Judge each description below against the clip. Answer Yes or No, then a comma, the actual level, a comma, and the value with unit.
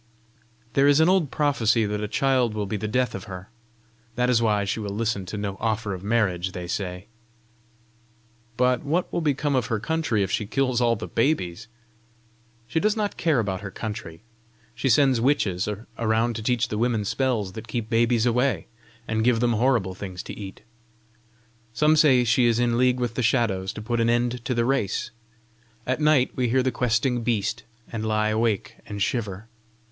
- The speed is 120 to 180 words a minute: No, average, 190 wpm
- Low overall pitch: Yes, low, 115 Hz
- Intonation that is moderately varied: Yes, average, 3.4 semitones